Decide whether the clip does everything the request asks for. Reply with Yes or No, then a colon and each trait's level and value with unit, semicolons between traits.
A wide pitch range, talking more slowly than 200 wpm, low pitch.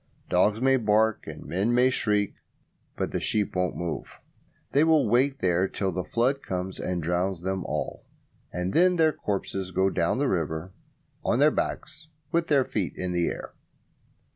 Yes: wide, 6.4 semitones; average, 170 wpm; low, 100 Hz